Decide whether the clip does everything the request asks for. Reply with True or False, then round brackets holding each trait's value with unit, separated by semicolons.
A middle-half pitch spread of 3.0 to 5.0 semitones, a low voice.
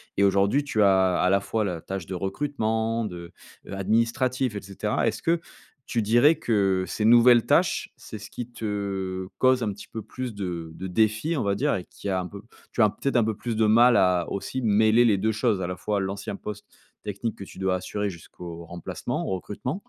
True (3.4 semitones; 105 Hz)